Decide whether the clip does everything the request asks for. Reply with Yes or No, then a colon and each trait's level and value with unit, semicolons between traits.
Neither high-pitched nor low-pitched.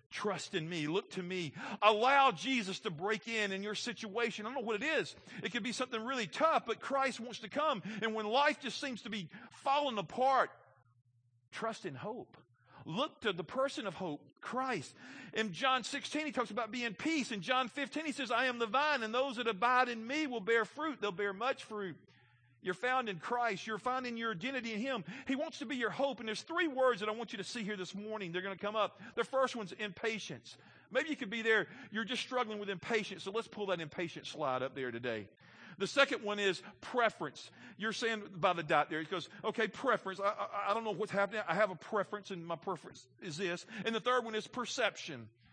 No: high, 220 Hz